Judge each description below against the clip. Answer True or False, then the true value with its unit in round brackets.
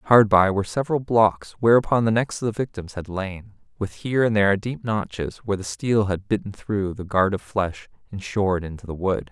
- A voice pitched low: True (100 Hz)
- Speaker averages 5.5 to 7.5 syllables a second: False (5.3 syllables/s)